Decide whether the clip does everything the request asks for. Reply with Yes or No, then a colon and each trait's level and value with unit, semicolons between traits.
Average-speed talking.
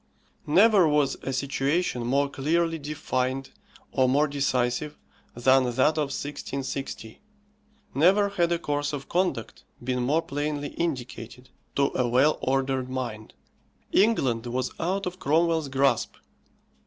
No: slow, 125 wpm